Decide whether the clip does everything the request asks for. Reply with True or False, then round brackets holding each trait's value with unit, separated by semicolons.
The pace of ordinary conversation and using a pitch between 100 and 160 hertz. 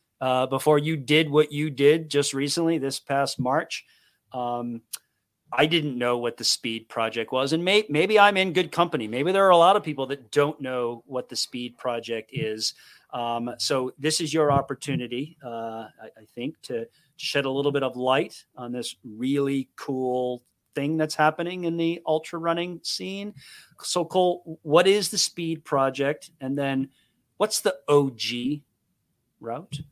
True (170 wpm; 140 Hz)